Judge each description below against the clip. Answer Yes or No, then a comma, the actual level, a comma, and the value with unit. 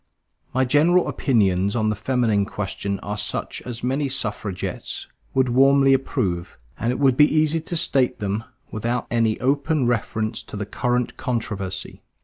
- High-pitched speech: No, low, 120 Hz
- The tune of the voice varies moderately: Yes, average, 4.6 semitones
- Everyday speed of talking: Yes, average, 150 wpm